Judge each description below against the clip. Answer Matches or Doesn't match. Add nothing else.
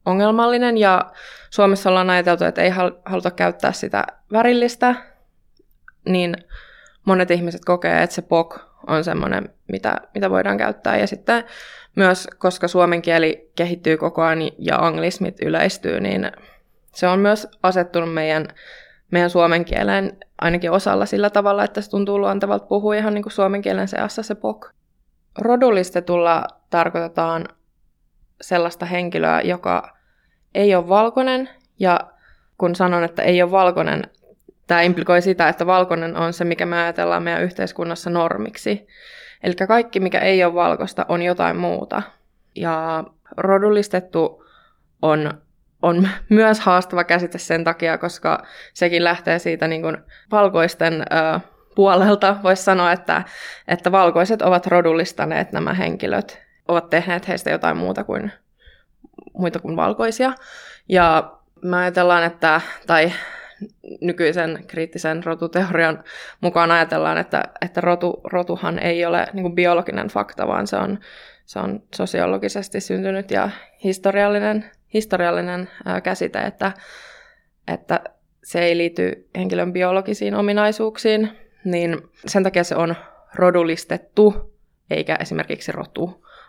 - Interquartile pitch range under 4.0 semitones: Matches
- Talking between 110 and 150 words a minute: Matches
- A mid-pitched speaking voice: Matches